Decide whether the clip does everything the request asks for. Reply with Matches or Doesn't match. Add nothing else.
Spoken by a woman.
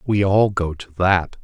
Doesn't match